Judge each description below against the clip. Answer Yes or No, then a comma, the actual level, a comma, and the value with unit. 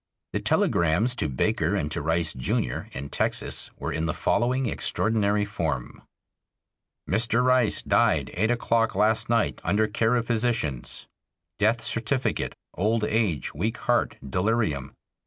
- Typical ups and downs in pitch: No, wide, 6.1 semitones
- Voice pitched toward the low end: Yes, low, 110 Hz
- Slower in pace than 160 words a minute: Yes, slow, 135 wpm